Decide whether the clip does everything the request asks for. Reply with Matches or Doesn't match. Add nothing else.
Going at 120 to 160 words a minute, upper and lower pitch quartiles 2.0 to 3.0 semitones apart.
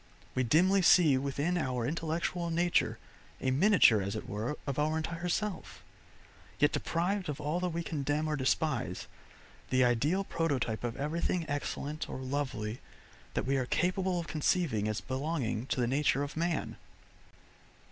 Doesn't match